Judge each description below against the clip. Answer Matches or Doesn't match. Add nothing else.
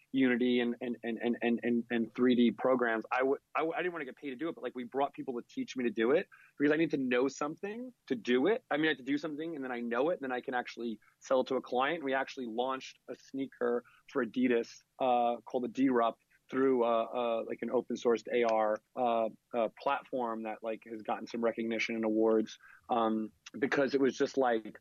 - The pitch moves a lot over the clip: Doesn't match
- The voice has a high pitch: Doesn't match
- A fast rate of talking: Matches